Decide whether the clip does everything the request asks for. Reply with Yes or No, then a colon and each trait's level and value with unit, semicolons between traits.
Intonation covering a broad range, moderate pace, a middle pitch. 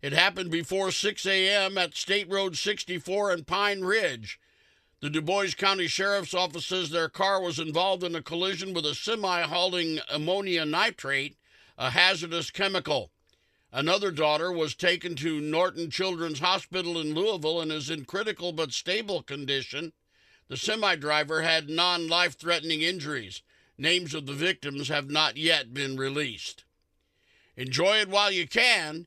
No: average, 3.4 semitones; average, 155 wpm; medium, 175 Hz